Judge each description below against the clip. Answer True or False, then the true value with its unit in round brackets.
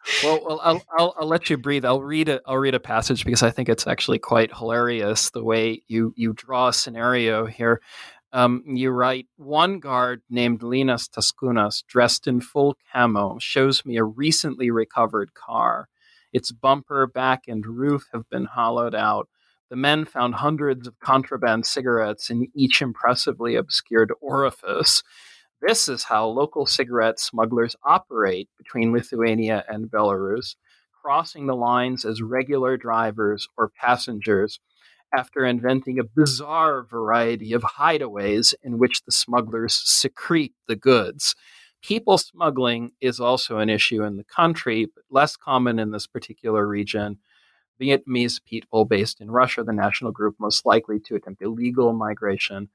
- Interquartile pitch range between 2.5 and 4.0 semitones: True (2.9 semitones)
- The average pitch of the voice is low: True (120 Hz)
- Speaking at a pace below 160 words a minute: True (150 wpm)